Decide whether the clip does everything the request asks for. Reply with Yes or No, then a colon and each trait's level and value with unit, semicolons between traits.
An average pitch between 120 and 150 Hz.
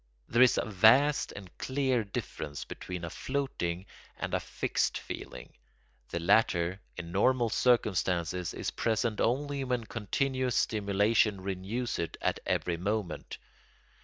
No: low, 105 Hz